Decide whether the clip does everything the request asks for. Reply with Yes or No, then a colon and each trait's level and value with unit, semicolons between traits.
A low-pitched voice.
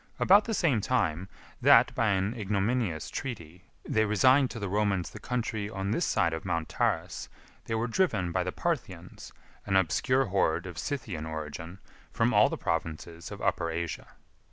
Yes: low, 100 Hz